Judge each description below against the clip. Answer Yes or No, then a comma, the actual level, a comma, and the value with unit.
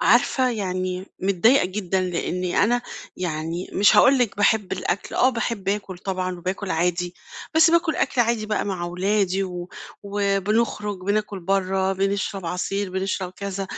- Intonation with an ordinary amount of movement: No, narrow, 2.3 semitones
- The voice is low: No, high, 195 Hz